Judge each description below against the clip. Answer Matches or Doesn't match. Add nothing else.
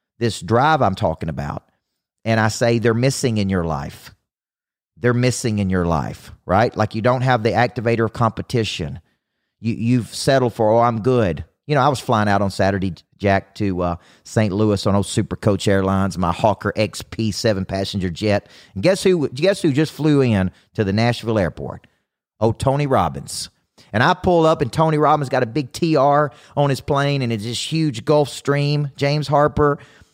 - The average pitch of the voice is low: Matches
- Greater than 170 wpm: Matches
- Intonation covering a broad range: Matches